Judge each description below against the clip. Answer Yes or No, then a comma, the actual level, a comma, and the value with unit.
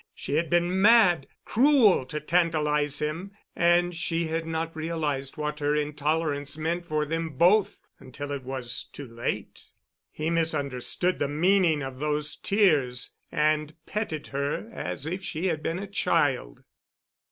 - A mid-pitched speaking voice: Yes, medium, 155 Hz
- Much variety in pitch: No, average, 3.0 semitones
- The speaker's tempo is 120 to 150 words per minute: Yes, average, 140 wpm